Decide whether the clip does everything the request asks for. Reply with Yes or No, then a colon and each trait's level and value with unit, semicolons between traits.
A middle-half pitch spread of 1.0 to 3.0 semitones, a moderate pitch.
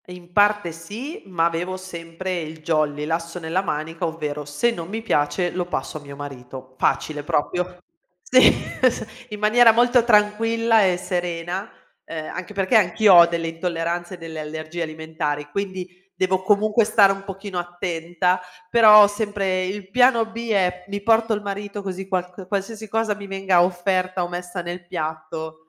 No: average, 3.7 semitones; medium, 180 Hz